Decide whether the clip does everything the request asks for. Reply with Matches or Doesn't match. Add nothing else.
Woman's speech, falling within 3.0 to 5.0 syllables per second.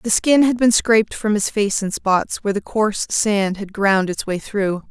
Matches